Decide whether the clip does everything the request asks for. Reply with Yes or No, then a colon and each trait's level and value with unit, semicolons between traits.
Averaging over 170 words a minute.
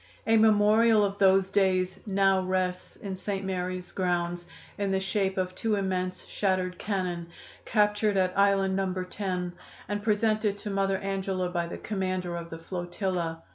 No: average, 155 wpm